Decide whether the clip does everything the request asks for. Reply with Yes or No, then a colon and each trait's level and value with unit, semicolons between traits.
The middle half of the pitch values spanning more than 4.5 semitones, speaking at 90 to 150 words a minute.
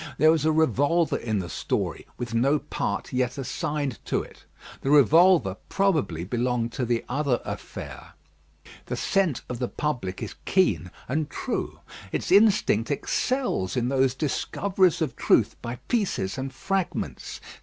Yes: average, 5.2 semitones; average, 145 wpm